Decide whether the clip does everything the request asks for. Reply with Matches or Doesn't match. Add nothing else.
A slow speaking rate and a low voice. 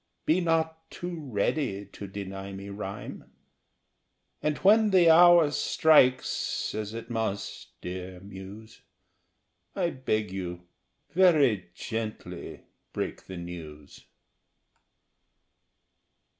Matches